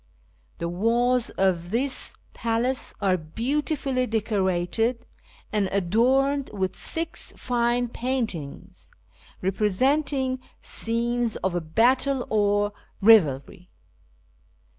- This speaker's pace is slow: Yes, slow, 85 wpm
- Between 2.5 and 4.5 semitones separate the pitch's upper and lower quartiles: No, average, 5.0 semitones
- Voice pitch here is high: Yes, high, 230 Hz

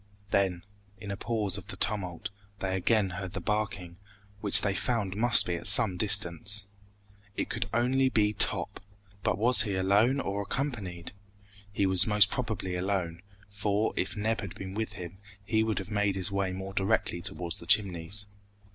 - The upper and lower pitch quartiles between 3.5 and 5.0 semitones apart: No, narrow, 2.4 semitones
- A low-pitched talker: Yes, low, 100 Hz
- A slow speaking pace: No, average, 175 wpm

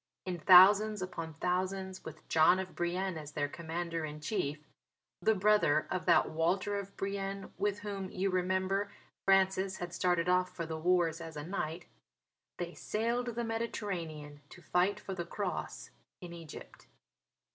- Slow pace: No, average, 150 wpm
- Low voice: No, medium, 185 Hz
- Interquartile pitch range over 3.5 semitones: No, average, 3.0 semitones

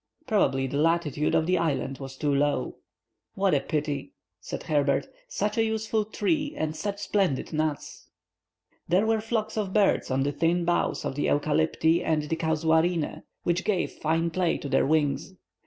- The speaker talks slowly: No, average, 170 wpm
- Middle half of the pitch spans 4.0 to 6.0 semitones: Yes, average, 4.9 semitones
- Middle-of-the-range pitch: Yes, medium, 160 Hz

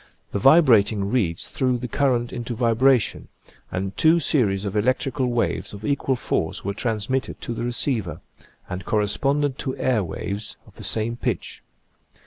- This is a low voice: Yes, low, 120 Hz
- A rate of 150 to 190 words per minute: Yes, average, 155 wpm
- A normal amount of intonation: Yes, average, 4.2 semitones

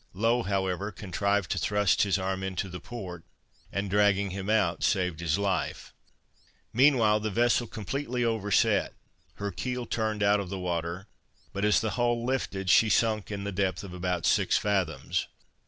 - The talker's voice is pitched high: No, low, 100 Hz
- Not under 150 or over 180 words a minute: Yes, average, 165 wpm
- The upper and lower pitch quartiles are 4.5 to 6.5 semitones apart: No, average, 2.8 semitones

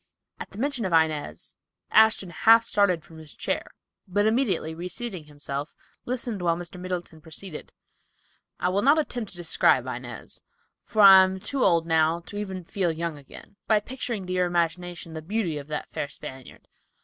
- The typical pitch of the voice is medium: Yes, medium, 180 Hz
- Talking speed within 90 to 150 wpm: No, average, 175 wpm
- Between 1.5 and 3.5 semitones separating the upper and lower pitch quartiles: No, average, 4.4 semitones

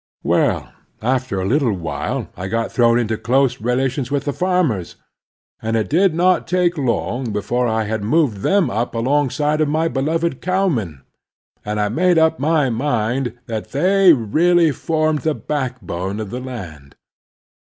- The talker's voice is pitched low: Yes, low, 130 Hz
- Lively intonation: Yes, wide, 6.1 semitones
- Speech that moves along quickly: No, average, 155 wpm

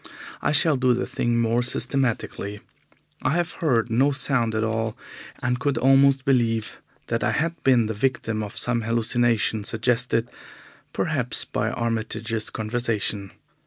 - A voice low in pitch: Yes, low, 120 Hz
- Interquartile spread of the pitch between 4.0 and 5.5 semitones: No, average, 2.8 semitones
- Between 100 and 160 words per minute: Yes, average, 140 wpm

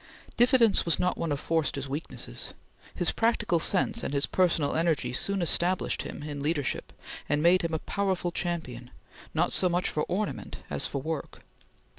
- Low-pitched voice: No, medium, 165 Hz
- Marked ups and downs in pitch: No, average, 4.0 semitones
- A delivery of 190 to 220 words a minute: No, average, 165 wpm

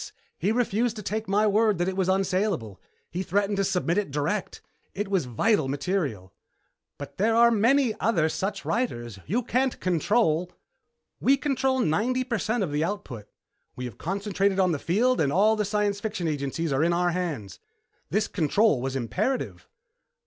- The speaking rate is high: No, average, 175 wpm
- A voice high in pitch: Yes, high, 195 Hz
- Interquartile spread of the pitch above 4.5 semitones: Yes, wide, 5.6 semitones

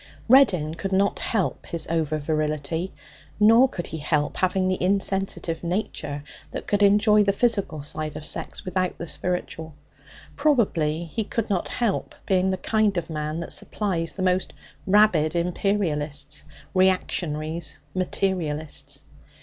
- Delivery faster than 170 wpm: No, slow, 135 wpm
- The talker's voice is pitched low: No, medium, 180 Hz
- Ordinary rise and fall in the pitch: Yes, average, 4.2 semitones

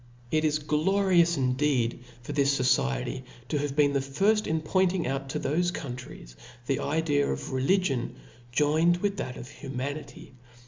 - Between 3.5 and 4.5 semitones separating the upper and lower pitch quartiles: Yes, average, 3.8 semitones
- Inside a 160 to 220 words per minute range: No, average, 150 wpm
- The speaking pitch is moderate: Yes, medium, 145 Hz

